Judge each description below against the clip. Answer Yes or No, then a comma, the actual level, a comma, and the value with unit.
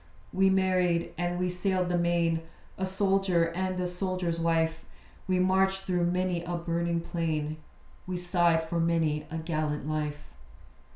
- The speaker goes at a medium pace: Yes, average, 150 wpm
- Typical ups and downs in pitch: No, narrow, 1.8 semitones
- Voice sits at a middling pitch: Yes, medium, 175 Hz